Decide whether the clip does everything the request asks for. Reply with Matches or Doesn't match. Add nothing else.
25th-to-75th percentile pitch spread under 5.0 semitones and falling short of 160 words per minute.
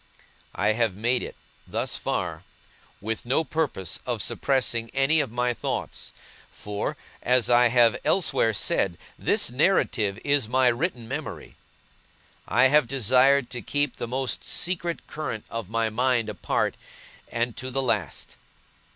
Matches